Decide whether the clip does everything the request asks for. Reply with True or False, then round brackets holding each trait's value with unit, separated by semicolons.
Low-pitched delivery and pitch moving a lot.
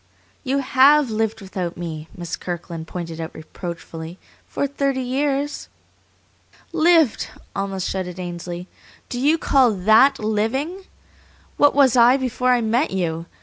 False (220 Hz; 7.6 semitones)